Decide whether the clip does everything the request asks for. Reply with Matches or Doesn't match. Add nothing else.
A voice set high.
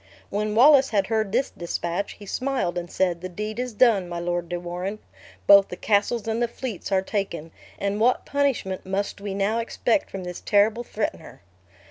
Matches